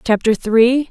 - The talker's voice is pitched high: Yes, high, 235 Hz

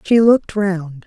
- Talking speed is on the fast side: No, average, 170 wpm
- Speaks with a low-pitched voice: No, high, 190 Hz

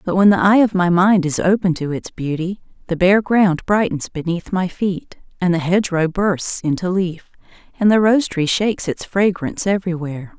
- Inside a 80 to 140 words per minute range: No, average, 195 wpm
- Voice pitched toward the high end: No, medium, 180 Hz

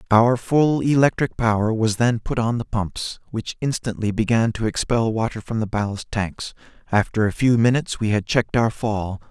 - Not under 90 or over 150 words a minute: No, average, 185 wpm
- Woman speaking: No, male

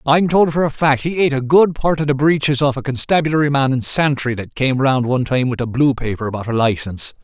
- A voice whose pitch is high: No, low, 135 Hz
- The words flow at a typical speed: No, fast, 255 wpm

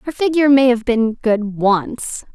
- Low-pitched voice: No, high, 240 Hz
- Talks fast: No, average, 180 wpm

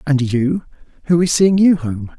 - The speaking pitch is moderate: Yes, medium, 150 Hz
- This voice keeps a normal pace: Yes, average, 190 wpm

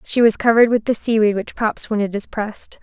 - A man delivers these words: No, female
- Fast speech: Yes, fast, 255 wpm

